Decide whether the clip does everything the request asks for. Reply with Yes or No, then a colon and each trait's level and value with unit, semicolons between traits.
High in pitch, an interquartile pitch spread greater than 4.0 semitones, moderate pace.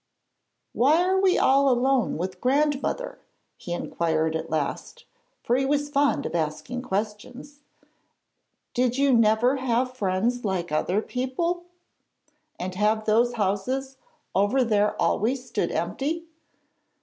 No: high, 245 Hz; average, 5.2 semitones; slow, 125 wpm